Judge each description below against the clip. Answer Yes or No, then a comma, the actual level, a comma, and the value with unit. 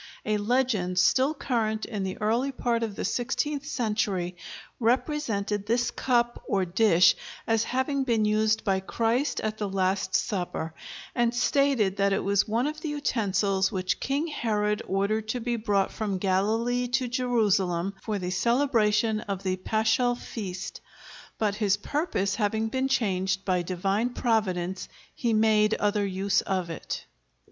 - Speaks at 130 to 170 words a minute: Yes, average, 150 wpm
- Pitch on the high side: Yes, high, 215 Hz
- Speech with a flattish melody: No, average, 3.7 semitones